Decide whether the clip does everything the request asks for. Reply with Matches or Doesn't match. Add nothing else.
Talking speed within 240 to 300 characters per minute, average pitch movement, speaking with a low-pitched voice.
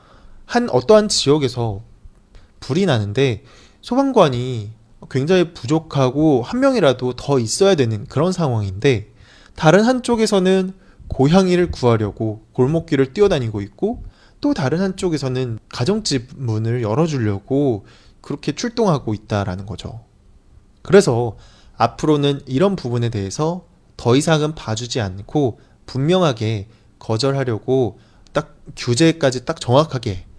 Doesn't match